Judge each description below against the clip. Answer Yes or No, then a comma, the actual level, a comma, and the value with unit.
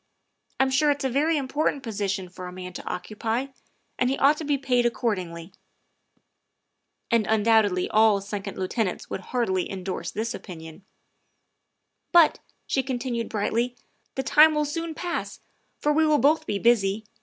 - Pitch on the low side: No, high, 230 Hz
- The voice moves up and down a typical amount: No, wide, 5.9 semitones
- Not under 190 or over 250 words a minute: No, average, 175 wpm